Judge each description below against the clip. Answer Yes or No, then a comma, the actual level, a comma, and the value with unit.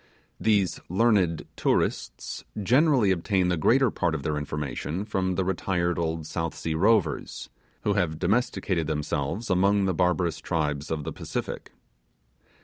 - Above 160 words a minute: No, slow, 135 wpm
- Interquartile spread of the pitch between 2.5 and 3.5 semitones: No, average, 4.0 semitones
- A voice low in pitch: Yes, very low, 90 Hz